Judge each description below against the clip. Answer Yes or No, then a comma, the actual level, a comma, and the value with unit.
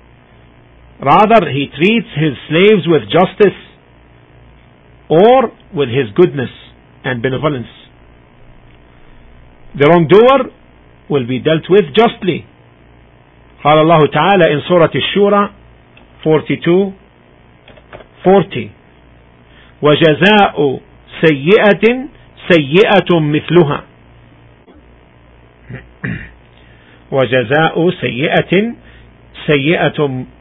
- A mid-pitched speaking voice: No, low, 130 Hz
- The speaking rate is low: Yes, slow, 70 wpm